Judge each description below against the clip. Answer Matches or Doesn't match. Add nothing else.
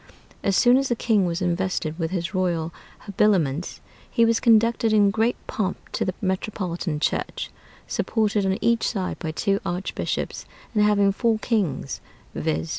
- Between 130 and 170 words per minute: Matches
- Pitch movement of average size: Matches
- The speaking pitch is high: Matches